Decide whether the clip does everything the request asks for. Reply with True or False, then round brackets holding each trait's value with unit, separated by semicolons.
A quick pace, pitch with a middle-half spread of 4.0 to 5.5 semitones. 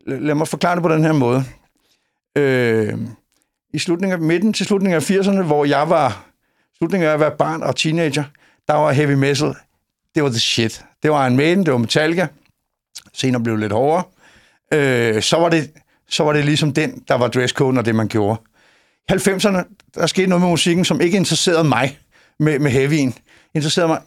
False (195 wpm; 4.3 semitones)